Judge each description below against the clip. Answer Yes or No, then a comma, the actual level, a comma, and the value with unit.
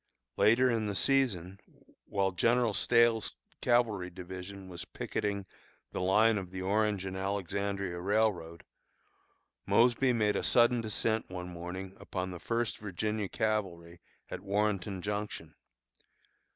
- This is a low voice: Yes, low, 100 Hz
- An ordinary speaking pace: No, slow, 125 wpm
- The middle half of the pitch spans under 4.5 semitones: Yes, average, 3.0 semitones